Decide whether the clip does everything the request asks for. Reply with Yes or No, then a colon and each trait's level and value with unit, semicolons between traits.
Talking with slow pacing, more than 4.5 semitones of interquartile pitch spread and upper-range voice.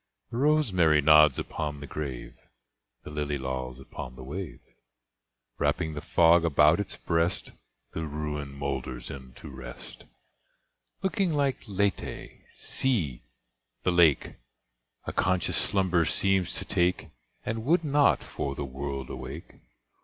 No: slow, 125 wpm; wide, 5.5 semitones; very low, 75 Hz